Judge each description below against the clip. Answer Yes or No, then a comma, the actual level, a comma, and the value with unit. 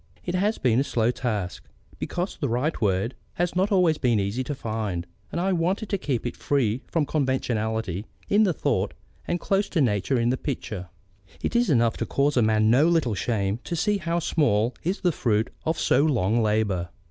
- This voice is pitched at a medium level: No, low, 130 Hz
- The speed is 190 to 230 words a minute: Yes, average, 195 wpm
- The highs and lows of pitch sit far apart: Yes, wide, 7.5 semitones